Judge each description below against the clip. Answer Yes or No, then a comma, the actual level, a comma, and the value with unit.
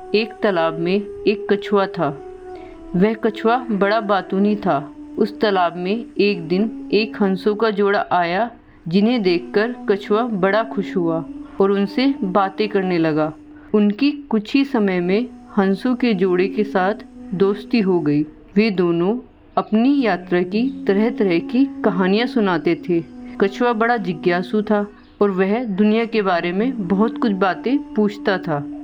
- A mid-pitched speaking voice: No, high, 210 Hz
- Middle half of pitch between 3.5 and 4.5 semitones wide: Yes, average, 3.8 semitones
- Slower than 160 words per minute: Yes, average, 150 wpm